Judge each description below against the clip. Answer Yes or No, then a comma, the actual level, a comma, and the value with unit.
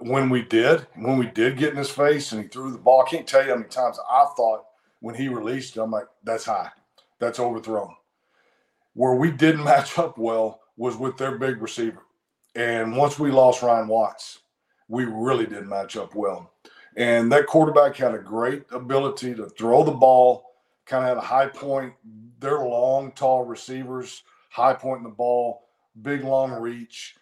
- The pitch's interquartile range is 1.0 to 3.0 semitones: Yes, narrow, 2.5 semitones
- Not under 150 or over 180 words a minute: No, average, 190 wpm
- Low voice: Yes, low, 125 Hz